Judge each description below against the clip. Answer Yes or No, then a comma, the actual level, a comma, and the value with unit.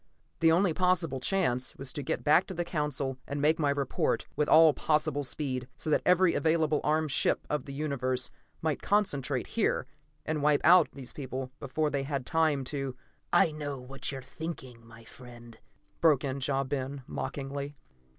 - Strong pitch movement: No, average, 3.0 semitones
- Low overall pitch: No, medium, 145 Hz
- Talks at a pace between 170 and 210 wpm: Yes, average, 180 wpm